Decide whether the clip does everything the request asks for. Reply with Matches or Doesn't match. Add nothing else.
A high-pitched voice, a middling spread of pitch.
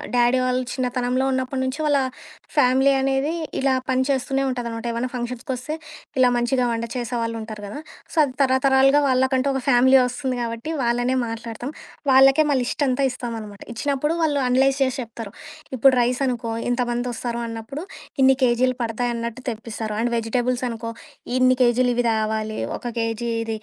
Doesn't match